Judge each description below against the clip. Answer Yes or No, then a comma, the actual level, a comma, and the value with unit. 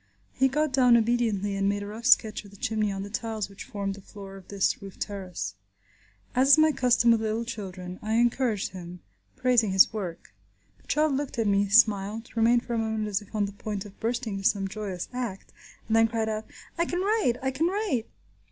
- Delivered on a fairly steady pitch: No, average, 3.5 semitones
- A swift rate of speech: Yes, fast, 215 wpm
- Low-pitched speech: No, high, 220 Hz